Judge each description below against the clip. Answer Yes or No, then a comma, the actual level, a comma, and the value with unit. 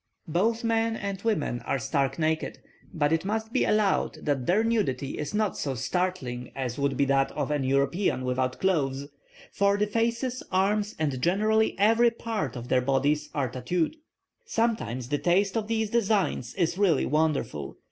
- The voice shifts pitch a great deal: Yes, wide, 7.7 semitones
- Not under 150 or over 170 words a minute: Yes, average, 165 wpm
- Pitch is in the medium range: Yes, medium, 170 Hz